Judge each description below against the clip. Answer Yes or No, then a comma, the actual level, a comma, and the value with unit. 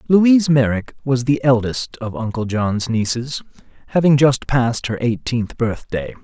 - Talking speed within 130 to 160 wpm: Yes, average, 145 wpm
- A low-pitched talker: Yes, low, 125 Hz